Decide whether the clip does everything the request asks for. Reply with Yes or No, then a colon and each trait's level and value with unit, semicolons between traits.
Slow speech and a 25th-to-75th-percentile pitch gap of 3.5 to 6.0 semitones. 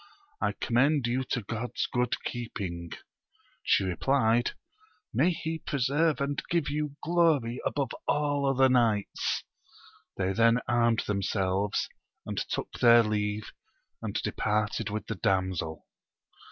Yes: slow, 120 wpm; average, 5.1 semitones